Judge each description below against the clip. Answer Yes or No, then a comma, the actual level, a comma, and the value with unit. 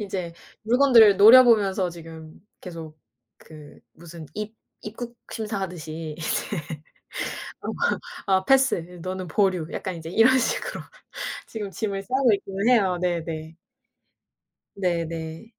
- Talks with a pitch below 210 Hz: Yes, high, 190 Hz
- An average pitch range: Yes, average, 5.0 semitones